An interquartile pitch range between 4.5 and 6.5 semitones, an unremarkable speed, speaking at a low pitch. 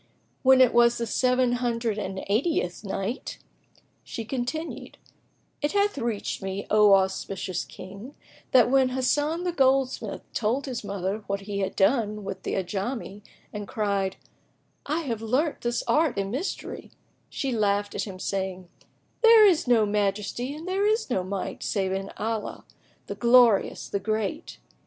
No: average, 4.8 semitones; average, 150 wpm; high, 225 Hz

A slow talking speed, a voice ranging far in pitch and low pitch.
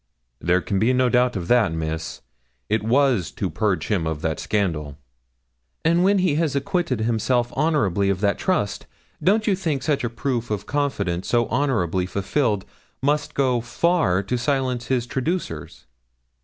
No: average, 160 wpm; wide, 6.5 semitones; low, 120 Hz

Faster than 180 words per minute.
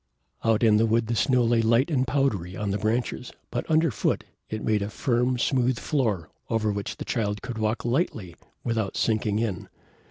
Yes: average, 190 wpm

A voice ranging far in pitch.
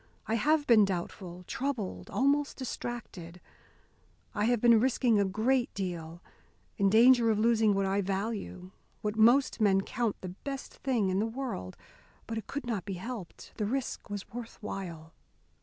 No: average, 4.0 semitones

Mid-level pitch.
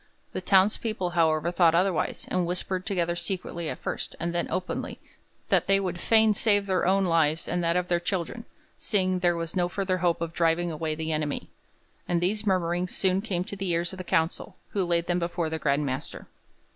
Yes: medium, 175 Hz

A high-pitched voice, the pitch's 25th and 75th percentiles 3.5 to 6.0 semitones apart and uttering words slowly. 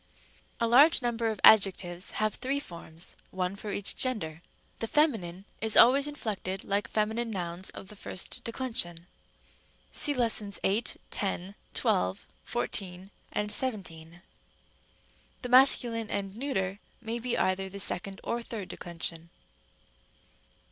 Yes: high, 205 Hz; average, 4.3 semitones; slow, 125 wpm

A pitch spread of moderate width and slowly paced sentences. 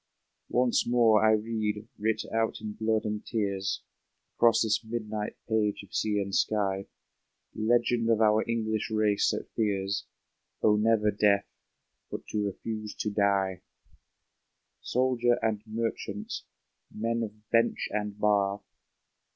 No: narrow, 1.6 semitones; slow, 125 wpm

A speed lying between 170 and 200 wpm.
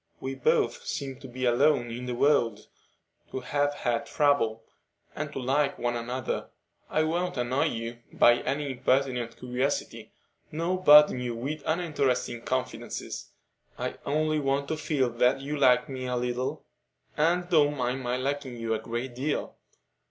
No: average, 155 wpm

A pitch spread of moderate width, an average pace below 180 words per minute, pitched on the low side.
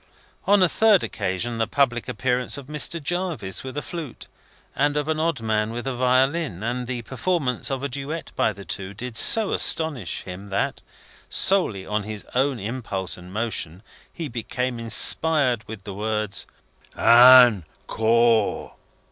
Yes: average, 4.9 semitones; average, 155 wpm; low, 125 Hz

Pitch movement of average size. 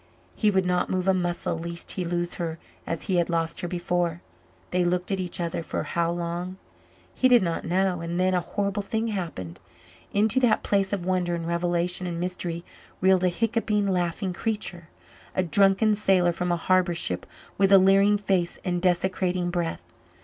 No: narrow, 2.0 semitones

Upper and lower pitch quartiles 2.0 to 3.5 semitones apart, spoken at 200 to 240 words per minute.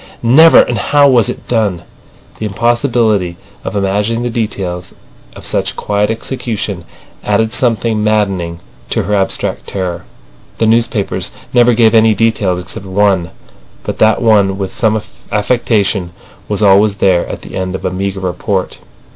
No: average, 3.0 semitones; average, 145 wpm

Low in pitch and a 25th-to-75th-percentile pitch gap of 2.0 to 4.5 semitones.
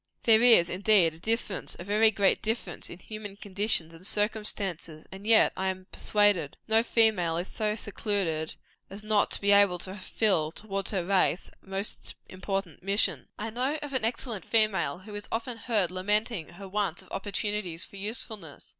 No: high, 200 Hz; average, 2.7 semitones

